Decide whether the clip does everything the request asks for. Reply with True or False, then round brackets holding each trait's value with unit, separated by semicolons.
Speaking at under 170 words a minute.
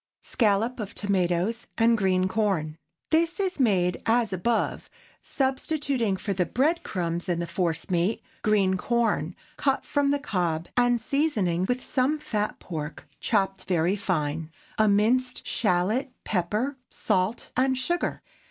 True (140 wpm)